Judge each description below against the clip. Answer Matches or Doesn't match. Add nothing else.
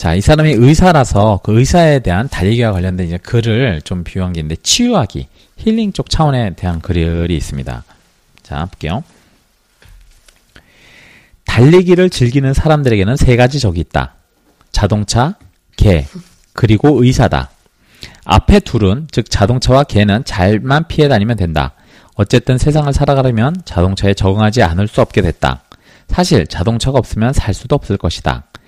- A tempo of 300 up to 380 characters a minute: Matches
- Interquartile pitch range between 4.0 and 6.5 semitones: Doesn't match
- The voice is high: Doesn't match